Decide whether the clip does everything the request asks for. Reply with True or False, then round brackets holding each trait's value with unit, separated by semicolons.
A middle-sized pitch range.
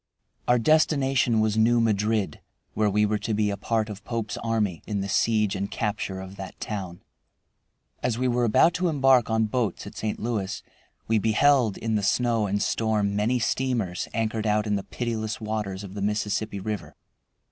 False (2.3 semitones)